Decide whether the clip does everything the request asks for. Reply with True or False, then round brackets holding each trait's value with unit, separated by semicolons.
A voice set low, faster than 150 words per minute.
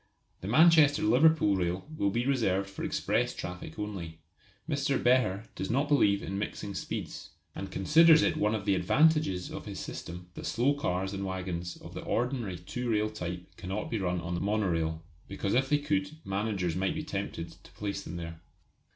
True (100 Hz; 185 wpm)